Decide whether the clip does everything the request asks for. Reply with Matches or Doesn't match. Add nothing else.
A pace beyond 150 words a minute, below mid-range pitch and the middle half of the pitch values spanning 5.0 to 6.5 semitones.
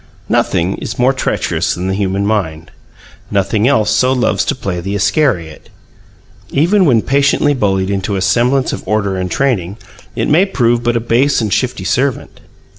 Matches